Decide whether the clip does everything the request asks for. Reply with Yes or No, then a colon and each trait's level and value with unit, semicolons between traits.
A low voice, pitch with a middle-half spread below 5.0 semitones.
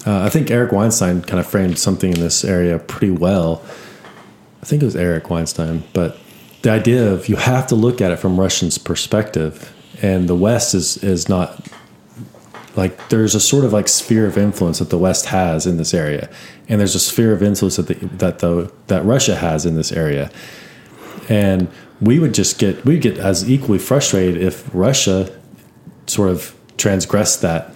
Yes: very low, 95 Hz; average, 3.4 semitones